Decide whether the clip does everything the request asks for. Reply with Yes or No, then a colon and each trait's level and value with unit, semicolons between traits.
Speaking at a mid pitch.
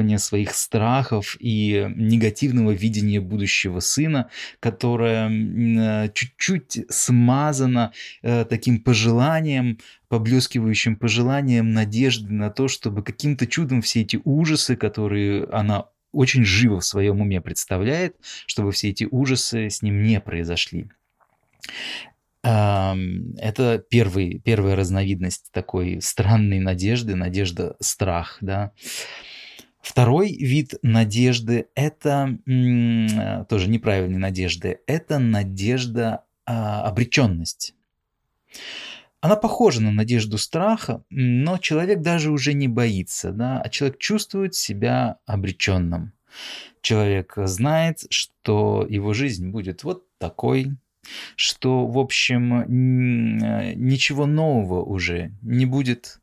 No: low, 115 Hz